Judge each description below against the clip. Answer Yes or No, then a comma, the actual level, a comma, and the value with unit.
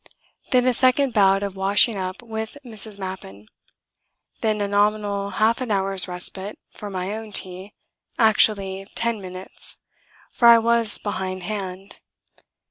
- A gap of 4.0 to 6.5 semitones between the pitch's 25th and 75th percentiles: No, narrow, 2.6 semitones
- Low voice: No, high, 205 Hz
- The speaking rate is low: Yes, slow, 130 wpm